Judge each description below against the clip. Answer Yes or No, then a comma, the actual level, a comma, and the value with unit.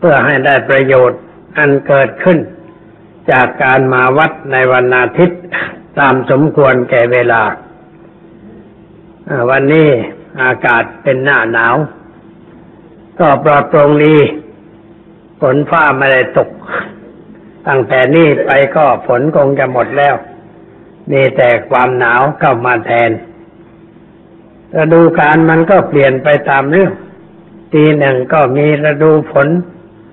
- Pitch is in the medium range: Yes, medium, 145 Hz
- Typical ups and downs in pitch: Yes, average, 3.6 semitones